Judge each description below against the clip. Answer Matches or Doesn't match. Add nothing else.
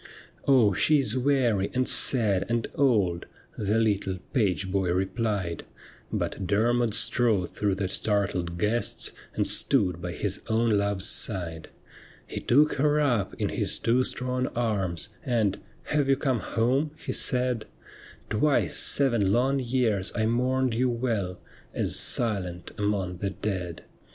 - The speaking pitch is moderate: Doesn't match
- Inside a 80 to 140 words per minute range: Doesn't match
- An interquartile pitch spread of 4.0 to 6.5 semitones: Matches